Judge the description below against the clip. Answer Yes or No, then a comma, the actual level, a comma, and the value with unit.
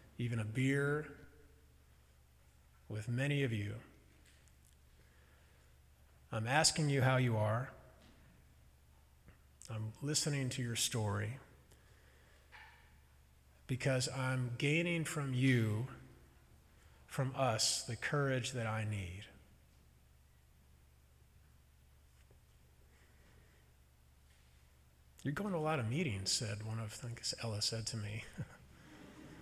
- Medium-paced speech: No, slow, 95 wpm